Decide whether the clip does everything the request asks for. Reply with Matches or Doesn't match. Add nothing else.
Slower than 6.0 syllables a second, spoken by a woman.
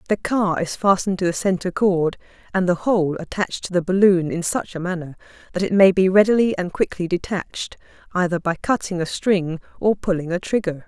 Matches